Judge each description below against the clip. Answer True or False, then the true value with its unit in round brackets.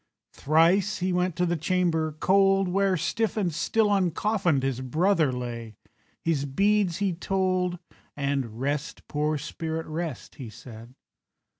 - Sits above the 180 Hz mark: False (165 Hz)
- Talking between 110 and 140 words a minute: True (135 wpm)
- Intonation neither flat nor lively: True (5.0 semitones)